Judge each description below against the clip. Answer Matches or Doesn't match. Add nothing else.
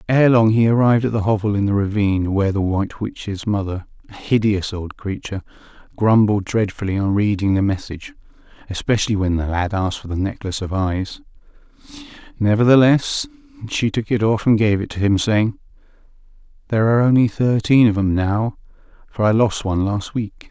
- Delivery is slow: Doesn't match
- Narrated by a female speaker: Doesn't match